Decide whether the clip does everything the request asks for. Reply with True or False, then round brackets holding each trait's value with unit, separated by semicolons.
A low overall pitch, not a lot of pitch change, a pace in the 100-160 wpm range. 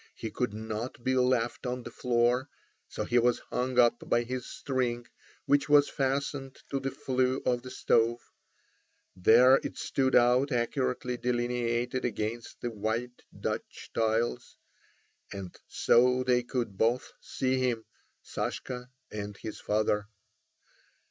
True (125 Hz; 1.6 semitones; 135 wpm)